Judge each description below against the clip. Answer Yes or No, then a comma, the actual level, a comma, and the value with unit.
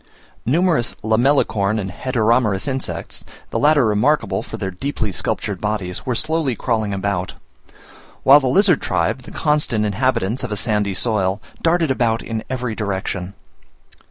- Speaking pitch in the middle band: No, low, 115 Hz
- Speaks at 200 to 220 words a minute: No, average, 140 wpm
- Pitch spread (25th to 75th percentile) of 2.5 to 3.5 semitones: No, average, 4.9 semitones